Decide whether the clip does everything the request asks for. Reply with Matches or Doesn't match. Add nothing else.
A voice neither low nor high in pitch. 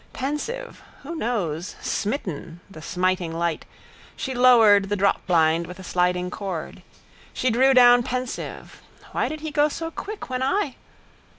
Doesn't match